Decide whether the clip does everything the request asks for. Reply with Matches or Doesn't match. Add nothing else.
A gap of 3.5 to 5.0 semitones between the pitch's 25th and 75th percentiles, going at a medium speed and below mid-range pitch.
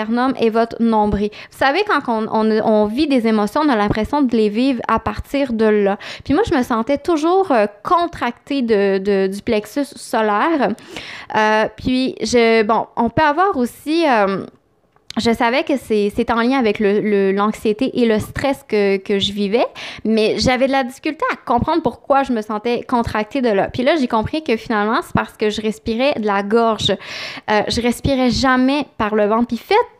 Doesn't match